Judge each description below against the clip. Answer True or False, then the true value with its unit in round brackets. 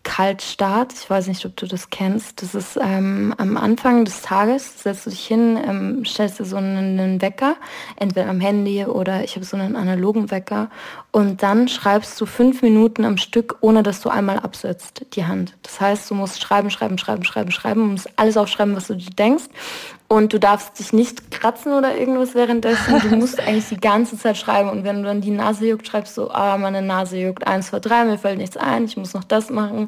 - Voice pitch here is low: False (210 Hz)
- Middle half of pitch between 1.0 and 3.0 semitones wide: True (2.7 semitones)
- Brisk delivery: True (220 wpm)